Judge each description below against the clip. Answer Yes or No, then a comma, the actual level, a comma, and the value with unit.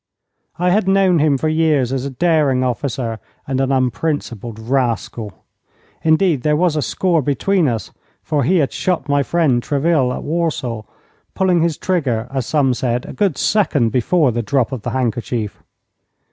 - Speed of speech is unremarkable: Yes, average, 165 wpm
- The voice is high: No, medium, 140 Hz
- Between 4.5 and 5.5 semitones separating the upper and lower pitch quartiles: Yes, average, 4.9 semitones